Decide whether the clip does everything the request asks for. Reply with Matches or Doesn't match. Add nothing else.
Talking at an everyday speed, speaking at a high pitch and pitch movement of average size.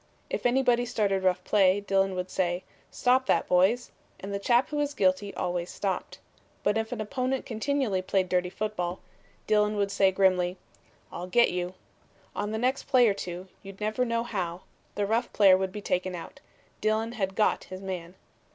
Matches